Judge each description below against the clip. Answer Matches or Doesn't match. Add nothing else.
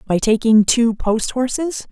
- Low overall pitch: Doesn't match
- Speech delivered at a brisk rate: Doesn't match